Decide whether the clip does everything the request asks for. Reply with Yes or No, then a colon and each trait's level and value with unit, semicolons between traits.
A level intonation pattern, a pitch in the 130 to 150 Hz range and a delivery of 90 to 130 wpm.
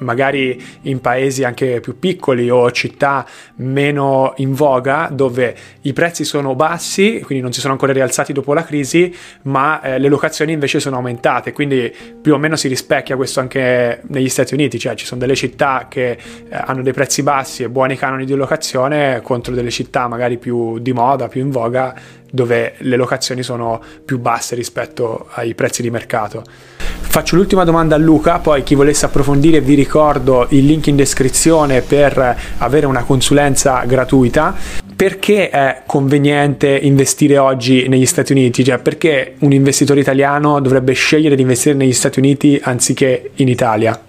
No: narrow, 2.3 semitones; low, 135 Hz; average, 165 wpm